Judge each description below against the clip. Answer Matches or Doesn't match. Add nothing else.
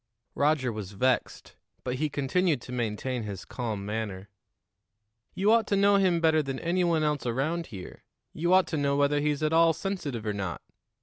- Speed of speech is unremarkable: Matches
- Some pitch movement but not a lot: Doesn't match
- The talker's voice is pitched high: Doesn't match